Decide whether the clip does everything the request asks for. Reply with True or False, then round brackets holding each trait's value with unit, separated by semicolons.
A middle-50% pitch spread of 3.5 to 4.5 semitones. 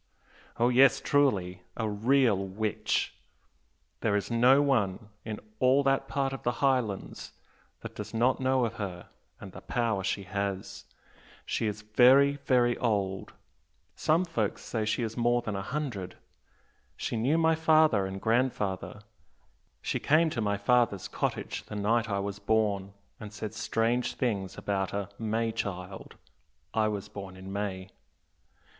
True (4.0 semitones)